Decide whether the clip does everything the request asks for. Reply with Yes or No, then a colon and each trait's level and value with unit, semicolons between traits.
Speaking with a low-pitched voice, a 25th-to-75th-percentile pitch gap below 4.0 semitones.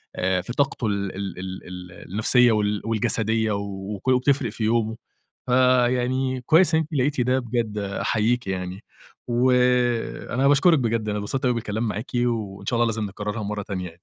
Yes: low, 115 Hz; average, 3.6 semitones